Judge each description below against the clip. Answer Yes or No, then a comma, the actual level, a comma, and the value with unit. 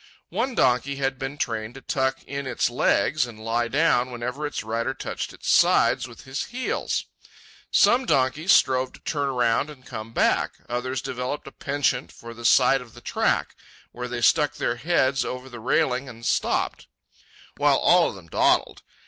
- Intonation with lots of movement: No, narrow, 2.5 semitones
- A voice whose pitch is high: No, low, 130 Hz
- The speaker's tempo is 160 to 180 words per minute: Yes, average, 175 wpm